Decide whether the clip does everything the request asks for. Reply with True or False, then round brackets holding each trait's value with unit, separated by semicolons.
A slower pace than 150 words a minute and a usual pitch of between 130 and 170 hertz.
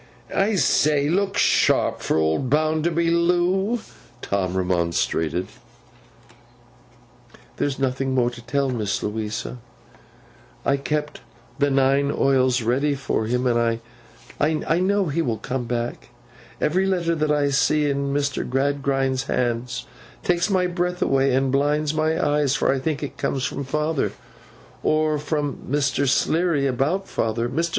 True (135 wpm; 140 Hz)